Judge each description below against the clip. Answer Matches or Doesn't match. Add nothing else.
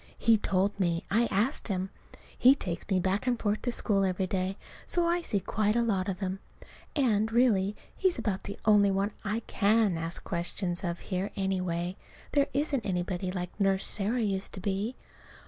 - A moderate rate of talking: Matches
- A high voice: Matches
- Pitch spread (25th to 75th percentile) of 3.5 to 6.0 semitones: Doesn't match